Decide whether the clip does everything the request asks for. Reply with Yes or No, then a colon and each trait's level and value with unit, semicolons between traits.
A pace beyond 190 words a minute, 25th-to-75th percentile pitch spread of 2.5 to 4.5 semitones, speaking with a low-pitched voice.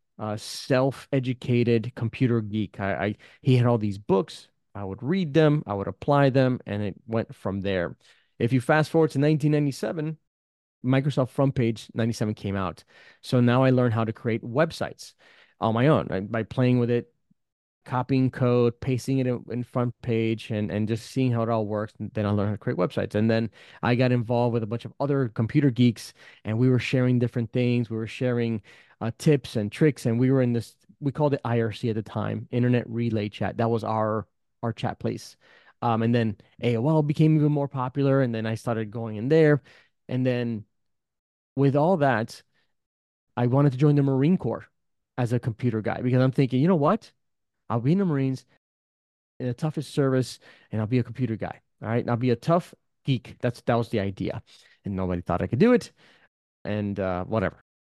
Yes: fast, 205 wpm; average, 3.2 semitones; low, 120 Hz